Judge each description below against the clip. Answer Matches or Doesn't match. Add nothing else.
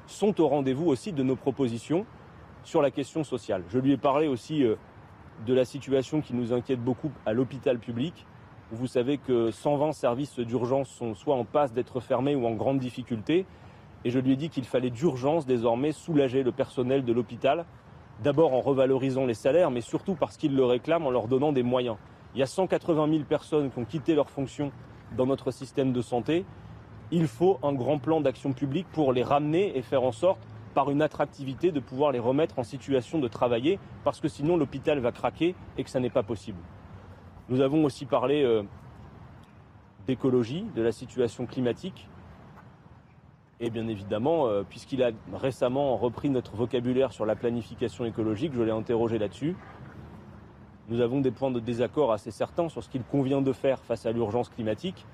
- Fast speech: Doesn't match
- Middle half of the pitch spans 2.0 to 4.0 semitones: Matches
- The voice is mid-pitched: Doesn't match